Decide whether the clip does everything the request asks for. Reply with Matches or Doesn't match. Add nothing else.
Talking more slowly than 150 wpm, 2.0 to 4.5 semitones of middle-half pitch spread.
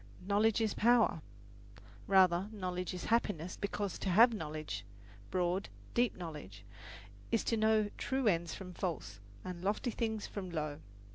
Matches